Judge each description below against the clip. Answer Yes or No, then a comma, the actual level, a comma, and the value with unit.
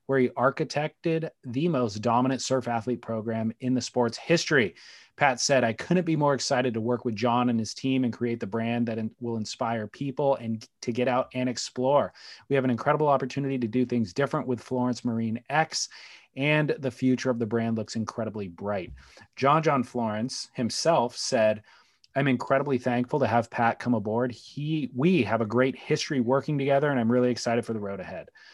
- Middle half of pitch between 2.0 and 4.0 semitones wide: Yes, average, 2.8 semitones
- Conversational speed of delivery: Yes, average, 195 wpm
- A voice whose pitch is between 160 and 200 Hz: No, low, 125 Hz